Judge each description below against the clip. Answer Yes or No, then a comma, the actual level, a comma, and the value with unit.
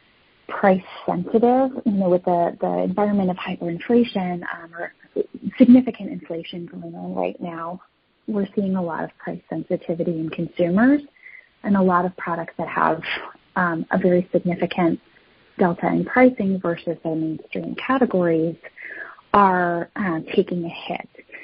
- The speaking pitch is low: No, medium, 180 Hz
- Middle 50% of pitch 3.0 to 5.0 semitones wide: Yes, average, 3.8 semitones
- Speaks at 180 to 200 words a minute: No, average, 140 wpm